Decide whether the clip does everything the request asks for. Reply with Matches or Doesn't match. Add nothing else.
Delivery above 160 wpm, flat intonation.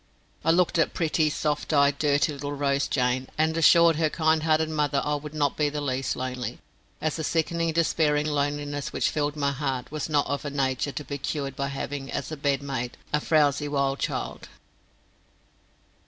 Matches